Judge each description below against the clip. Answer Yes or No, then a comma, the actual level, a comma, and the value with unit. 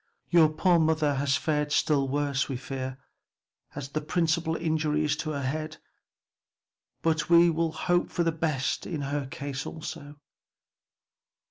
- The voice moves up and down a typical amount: No, narrow, 2.3 semitones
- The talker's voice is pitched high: No, medium, 155 Hz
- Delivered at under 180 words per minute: Yes, average, 145 wpm